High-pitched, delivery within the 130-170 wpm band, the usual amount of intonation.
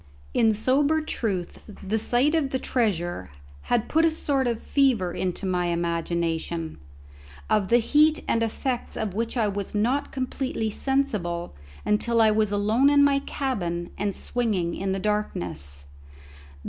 No: high, 215 Hz; average, 145 wpm; wide, 6.4 semitones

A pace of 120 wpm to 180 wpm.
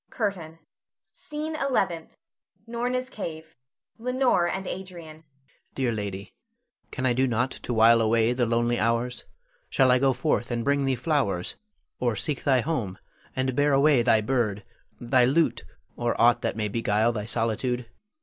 Yes: average, 160 wpm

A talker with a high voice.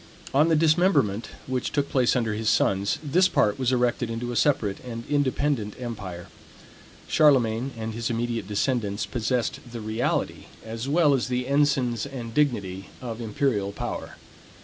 No: low, 120 Hz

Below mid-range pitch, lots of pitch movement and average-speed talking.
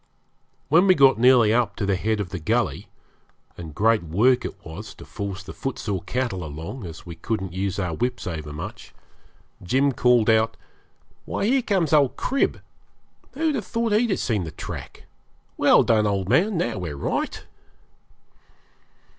Yes: low, 110 Hz; wide, 6.7 semitones; average, 165 wpm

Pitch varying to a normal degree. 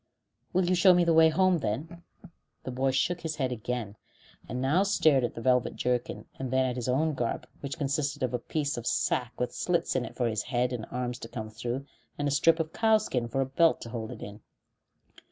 Yes: average, 4.7 semitones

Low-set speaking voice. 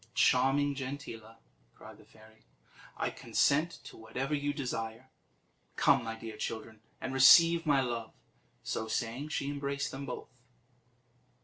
Yes: low, 130 Hz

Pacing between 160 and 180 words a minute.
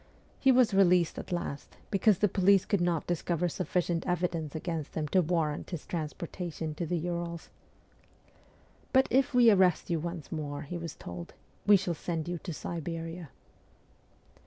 Yes: average, 165 wpm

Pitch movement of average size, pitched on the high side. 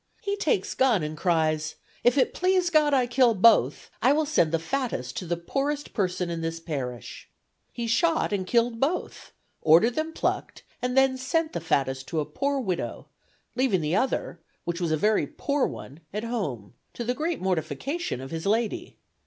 No: wide, 8.8 semitones; high, 225 Hz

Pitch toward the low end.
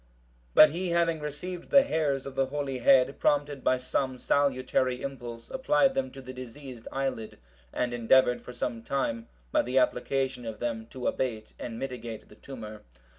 Yes: low, 130 Hz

